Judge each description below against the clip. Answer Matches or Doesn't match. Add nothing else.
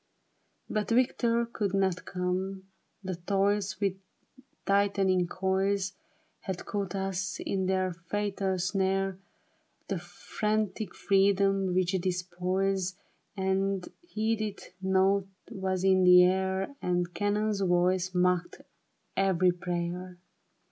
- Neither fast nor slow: Doesn't match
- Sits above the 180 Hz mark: Matches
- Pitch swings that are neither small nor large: Doesn't match